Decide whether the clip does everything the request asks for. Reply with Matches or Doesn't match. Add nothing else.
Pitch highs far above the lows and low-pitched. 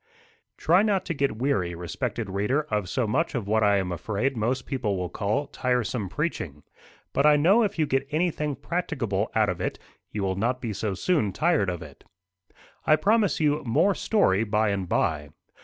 Matches